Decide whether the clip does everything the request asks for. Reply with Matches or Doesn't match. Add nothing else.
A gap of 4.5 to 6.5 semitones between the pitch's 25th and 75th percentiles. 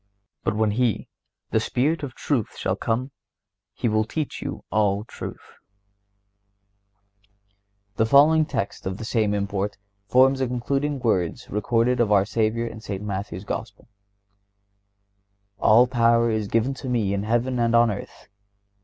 Doesn't match